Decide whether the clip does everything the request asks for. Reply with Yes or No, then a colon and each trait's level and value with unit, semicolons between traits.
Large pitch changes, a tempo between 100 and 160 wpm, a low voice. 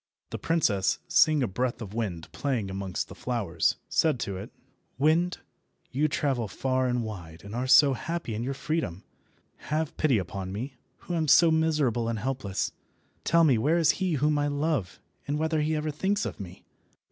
No: wide, 6.4 semitones; average, 180 wpm; low, 130 Hz